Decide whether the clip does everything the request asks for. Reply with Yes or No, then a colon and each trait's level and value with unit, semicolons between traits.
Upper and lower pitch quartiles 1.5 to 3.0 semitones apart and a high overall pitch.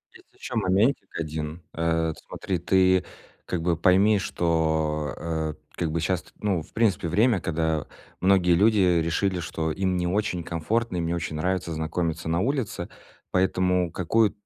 No: average, 2.7 semitones; very low, 90 Hz